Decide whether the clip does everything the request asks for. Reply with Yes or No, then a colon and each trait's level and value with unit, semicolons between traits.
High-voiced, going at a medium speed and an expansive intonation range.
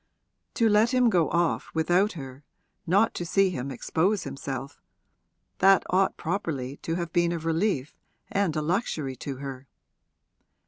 No: medium, 170 Hz; average, 145 wpm; wide, 5.7 semitones